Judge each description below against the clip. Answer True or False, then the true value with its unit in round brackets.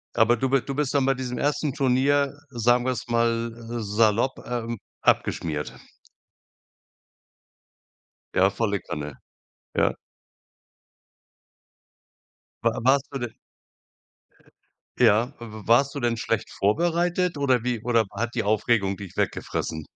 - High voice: False (120 Hz)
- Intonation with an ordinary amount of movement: True (3.5 semitones)